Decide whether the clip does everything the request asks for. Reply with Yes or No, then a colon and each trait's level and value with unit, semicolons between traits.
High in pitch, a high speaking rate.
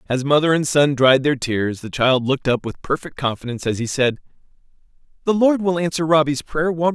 No: medium, 145 Hz; fast, 215 wpm